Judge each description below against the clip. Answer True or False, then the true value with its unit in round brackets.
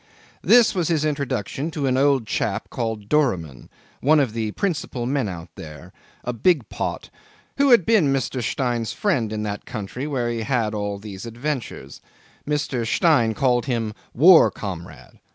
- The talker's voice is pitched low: True (125 Hz)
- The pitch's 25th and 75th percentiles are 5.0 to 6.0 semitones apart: True (5.5 semitones)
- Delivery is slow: False (160 wpm)